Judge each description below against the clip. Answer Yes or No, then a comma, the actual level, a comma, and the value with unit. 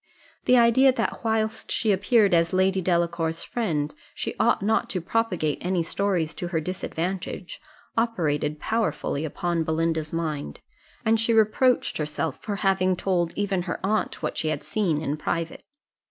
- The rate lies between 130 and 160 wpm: Yes, average, 155 wpm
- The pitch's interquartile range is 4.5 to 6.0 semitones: Yes, average, 4.9 semitones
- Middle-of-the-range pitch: Yes, medium, 180 Hz